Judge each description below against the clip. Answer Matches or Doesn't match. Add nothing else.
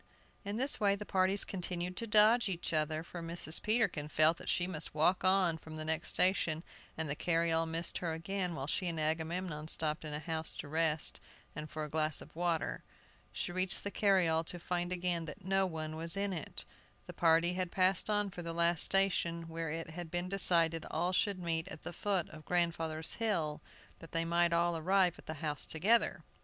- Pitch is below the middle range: Doesn't match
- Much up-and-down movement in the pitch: Doesn't match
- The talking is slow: Doesn't match